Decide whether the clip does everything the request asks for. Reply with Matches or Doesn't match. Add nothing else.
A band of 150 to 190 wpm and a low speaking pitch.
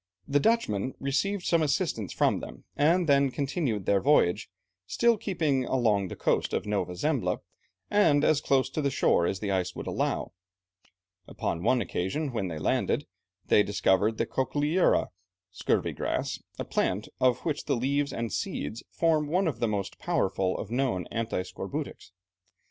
Matches